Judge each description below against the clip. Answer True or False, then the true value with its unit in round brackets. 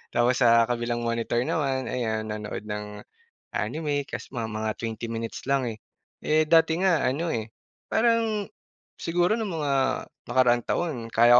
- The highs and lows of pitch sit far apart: True (5.7 semitones)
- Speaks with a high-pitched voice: False (125 Hz)